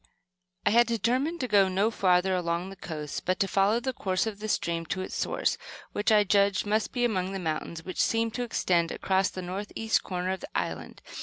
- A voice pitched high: Yes, high, 195 Hz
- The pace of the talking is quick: Yes, fast, 215 wpm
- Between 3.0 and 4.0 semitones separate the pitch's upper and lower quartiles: Yes, average, 3.4 semitones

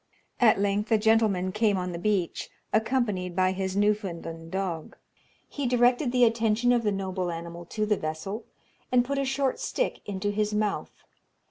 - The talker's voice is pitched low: No, high, 210 Hz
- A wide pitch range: No, average, 3.8 semitones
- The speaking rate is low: No, average, 165 wpm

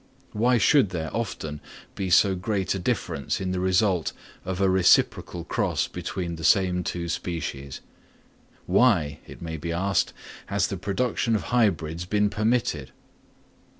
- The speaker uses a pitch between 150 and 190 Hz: No, very low, 95 Hz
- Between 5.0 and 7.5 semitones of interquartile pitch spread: No, average, 3.4 semitones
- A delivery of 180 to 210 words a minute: No, average, 150 wpm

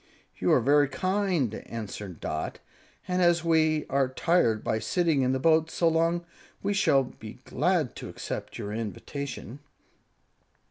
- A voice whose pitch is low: No, medium, 145 Hz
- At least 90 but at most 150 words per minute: Yes, average, 145 wpm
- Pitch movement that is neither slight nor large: No, wide, 6.5 semitones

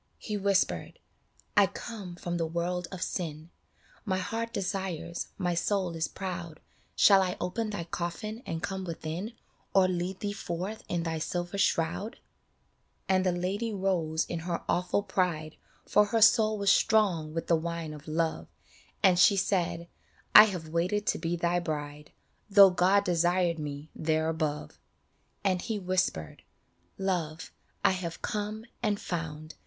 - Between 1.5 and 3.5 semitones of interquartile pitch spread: Yes, average, 3.1 semitones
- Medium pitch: Yes, medium, 180 Hz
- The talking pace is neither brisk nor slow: Yes, average, 160 wpm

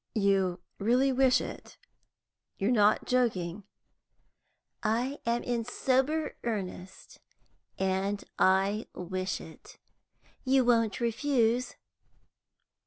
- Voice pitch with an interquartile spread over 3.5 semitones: Yes, average, 4.7 semitones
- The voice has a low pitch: No, high, 225 Hz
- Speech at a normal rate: No, slow, 95 wpm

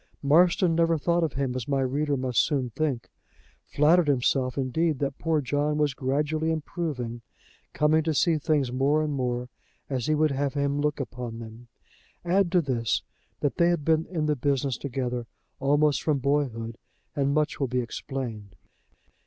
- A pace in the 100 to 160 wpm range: No, average, 170 wpm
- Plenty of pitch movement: No, average, 3.2 semitones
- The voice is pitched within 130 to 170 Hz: Yes, medium, 140 Hz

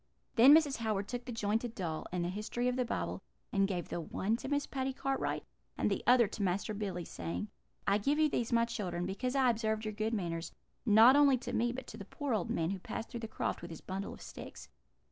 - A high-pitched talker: Yes, high, 220 Hz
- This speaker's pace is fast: Yes, fast, 240 wpm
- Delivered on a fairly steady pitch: No, average, 4.2 semitones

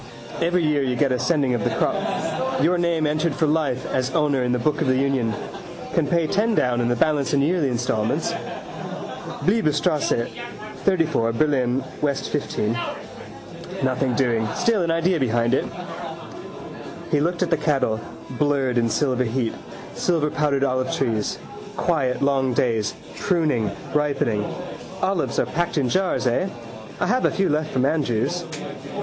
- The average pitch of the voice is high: No, medium, 140 Hz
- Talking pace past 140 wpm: Yes, average, 150 wpm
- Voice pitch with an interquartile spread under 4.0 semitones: No, average, 4.5 semitones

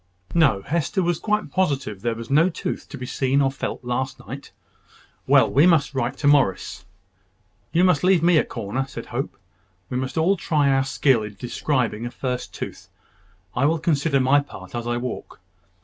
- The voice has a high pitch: No, low, 135 Hz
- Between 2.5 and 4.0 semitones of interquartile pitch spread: No, average, 4.7 semitones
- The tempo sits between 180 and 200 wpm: Yes, average, 185 wpm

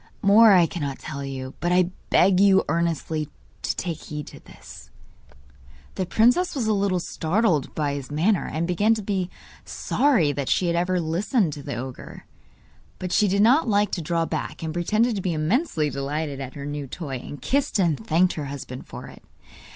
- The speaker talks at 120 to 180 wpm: No, average, 190 wpm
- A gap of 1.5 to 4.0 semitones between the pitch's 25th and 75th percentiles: No, wide, 5.4 semitones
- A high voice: No, medium, 170 Hz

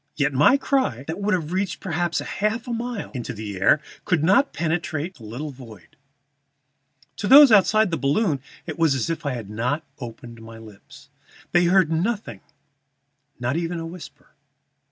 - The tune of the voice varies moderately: No, wide, 7.0 semitones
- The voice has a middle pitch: Yes, medium, 165 Hz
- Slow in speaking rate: No, average, 165 wpm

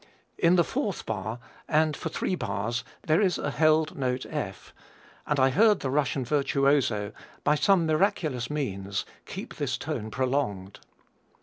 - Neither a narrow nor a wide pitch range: Yes, average, 4.9 semitones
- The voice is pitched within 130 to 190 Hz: Yes, medium, 140 Hz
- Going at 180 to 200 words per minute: No, average, 145 wpm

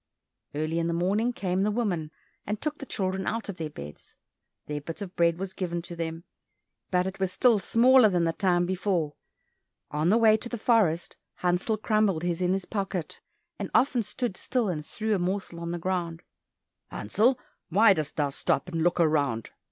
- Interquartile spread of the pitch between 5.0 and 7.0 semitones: No, average, 4.1 semitones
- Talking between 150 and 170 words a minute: No, average, 190 wpm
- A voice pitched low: No, medium, 185 Hz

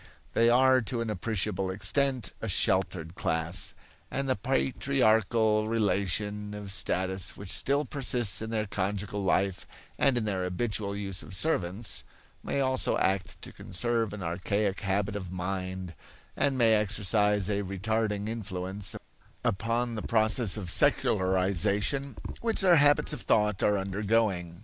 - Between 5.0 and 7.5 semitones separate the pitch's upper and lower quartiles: No, average, 3.3 semitones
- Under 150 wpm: Yes, average, 140 wpm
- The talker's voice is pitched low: Yes, low, 105 Hz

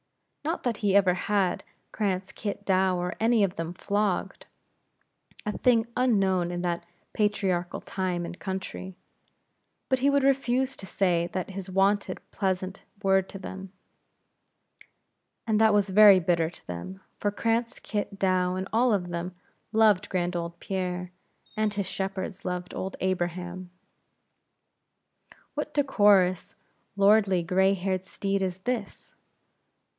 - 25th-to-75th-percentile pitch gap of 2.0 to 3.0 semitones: Yes, narrow, 2.4 semitones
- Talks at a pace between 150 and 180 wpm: No, slow, 135 wpm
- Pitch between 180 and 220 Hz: Yes, high, 190 Hz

